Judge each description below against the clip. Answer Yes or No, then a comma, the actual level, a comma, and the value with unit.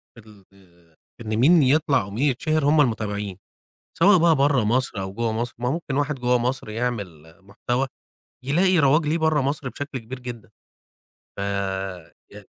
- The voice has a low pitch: Yes, low, 125 Hz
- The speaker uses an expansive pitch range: Yes, wide, 5.9 semitones